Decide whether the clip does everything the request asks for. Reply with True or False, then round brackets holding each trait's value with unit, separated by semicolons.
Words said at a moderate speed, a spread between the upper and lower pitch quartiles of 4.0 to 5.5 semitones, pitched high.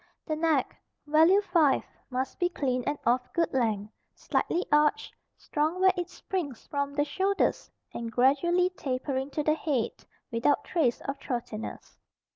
True (145 wpm; 4.9 semitones; 290 Hz)